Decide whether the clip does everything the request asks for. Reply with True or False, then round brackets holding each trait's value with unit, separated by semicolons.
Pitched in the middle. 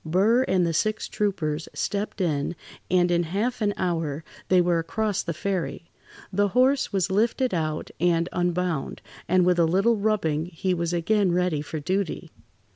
True (180 Hz)